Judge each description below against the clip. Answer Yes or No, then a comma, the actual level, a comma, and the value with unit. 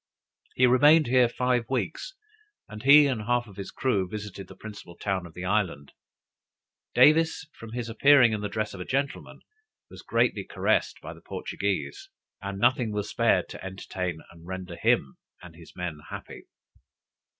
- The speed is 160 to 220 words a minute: Yes, average, 165 wpm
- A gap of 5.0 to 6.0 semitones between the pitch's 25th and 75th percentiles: Yes, wide, 5.4 semitones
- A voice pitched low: Yes, low, 105 Hz